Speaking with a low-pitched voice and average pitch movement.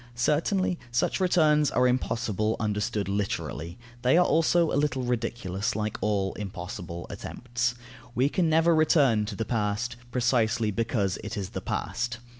Yes: low, 120 Hz; average, 4.8 semitones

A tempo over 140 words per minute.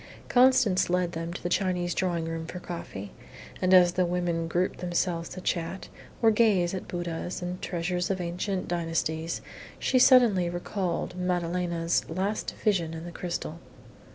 Yes: average, 155 wpm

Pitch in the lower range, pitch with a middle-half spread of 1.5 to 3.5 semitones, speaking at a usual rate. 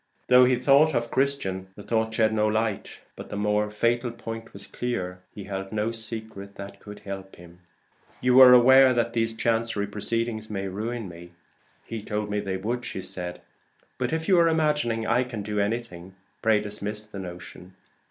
Yes: low, 110 Hz; average, 3.0 semitones; average, 175 wpm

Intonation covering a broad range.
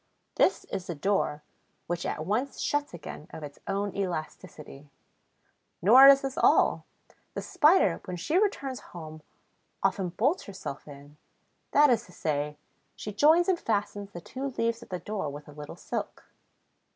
Yes: wide, 8.9 semitones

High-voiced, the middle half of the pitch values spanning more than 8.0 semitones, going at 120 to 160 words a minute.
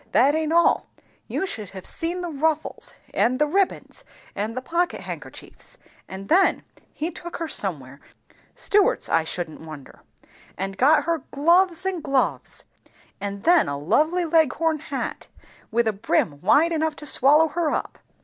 Yes: very high, 300 Hz; wide, 8.7 semitones; average, 150 wpm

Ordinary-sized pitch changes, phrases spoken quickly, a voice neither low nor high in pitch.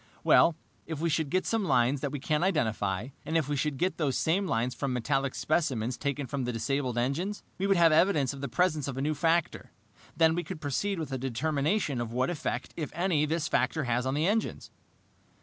Yes: average, 4.2 semitones; fast, 215 wpm; medium, 145 Hz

